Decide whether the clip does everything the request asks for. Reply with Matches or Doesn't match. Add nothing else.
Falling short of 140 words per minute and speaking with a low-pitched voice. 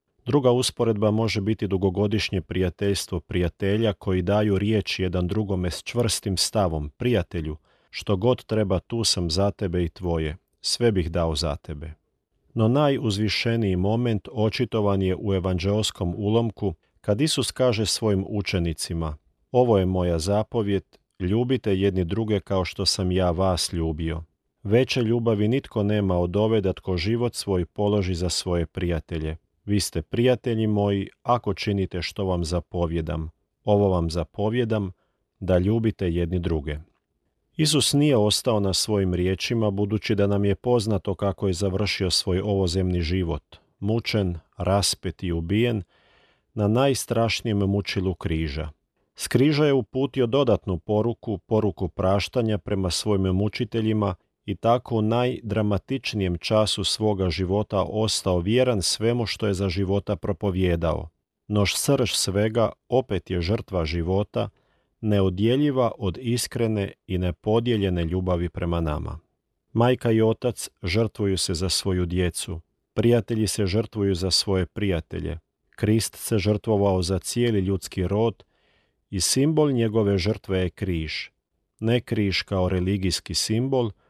Matches